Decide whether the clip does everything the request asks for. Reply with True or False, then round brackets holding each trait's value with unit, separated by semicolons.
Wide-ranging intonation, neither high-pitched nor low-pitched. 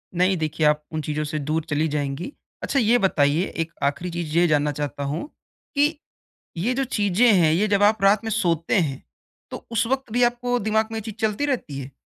True (6.5 semitones; 180 Hz)